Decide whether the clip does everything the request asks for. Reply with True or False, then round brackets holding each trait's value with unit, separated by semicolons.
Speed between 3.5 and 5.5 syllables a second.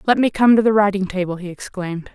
False (6.4 syllables/s)